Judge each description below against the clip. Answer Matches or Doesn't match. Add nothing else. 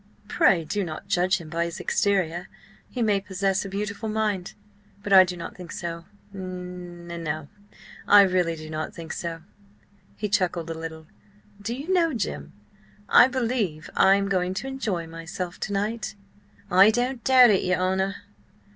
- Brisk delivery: Doesn't match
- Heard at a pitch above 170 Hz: Matches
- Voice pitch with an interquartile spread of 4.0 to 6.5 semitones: Doesn't match